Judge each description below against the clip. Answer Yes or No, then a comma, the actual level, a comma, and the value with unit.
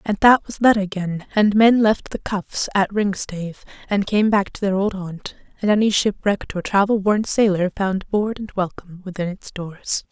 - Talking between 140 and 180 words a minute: No, average, 195 wpm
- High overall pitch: Yes, high, 200 Hz